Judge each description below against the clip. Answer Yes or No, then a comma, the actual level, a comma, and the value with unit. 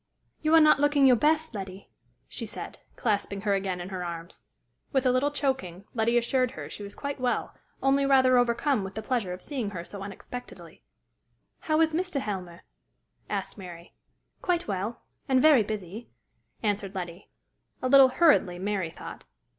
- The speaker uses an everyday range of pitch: No, wide, 6.1 semitones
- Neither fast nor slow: Yes, average, 170 wpm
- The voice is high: Yes, high, 230 Hz